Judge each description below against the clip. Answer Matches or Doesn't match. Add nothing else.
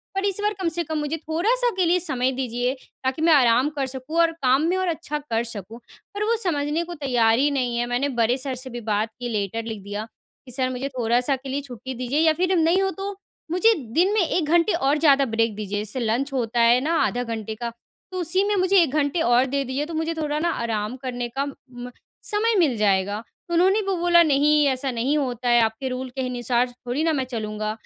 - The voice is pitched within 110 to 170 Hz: Doesn't match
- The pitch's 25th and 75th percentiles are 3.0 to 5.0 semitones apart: Doesn't match